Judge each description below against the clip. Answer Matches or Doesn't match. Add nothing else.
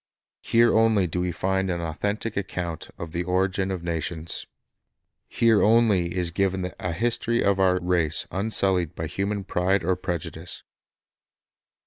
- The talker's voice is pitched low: Matches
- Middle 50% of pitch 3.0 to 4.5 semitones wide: Doesn't match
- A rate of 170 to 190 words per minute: Doesn't match